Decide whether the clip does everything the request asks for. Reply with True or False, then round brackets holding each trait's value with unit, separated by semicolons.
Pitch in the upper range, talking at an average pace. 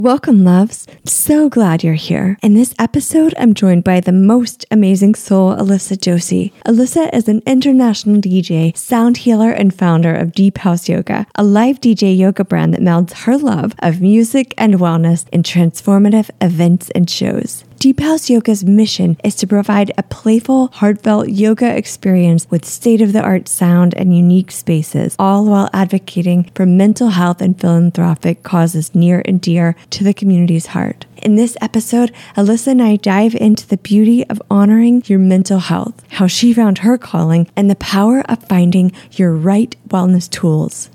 True (200 Hz; 170 wpm)